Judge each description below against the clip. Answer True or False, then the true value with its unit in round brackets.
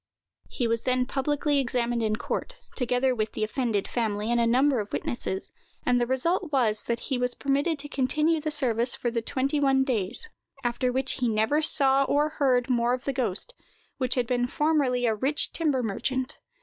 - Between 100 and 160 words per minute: False (190 wpm)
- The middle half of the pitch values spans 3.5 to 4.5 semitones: False (2.9 semitones)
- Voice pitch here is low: False (255 Hz)